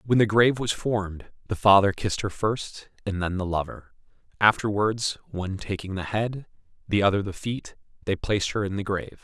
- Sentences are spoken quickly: No, average, 190 wpm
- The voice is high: No, low, 100 Hz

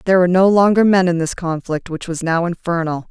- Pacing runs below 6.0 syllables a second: No, 6.1 syllables/s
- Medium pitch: Yes, medium, 175 Hz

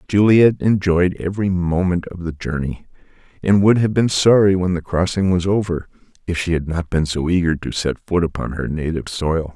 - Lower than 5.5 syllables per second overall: Yes, 5.2 syllables/s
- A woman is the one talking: No, male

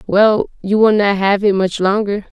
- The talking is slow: No, average, 200 wpm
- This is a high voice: Yes, high, 200 Hz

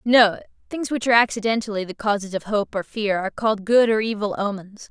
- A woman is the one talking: Yes, female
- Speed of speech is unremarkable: Yes, average, 195 wpm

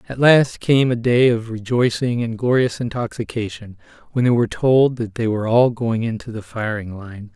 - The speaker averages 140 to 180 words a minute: No, average, 190 wpm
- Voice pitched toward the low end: Yes, low, 115 Hz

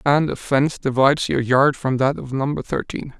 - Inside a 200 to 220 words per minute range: Yes, fast, 205 wpm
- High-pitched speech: No, low, 135 Hz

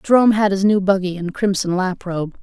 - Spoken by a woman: Yes, female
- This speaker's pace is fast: Yes, fast, 225 wpm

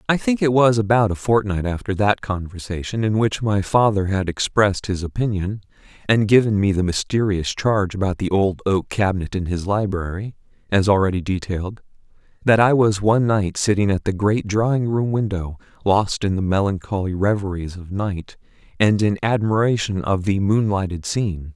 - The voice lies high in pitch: No, low, 100 Hz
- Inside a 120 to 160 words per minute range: No, average, 170 wpm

